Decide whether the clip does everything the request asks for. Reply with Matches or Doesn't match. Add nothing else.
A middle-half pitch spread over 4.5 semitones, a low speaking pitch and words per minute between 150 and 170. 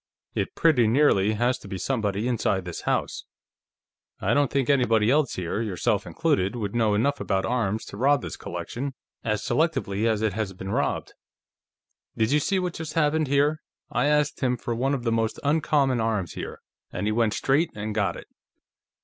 Doesn't match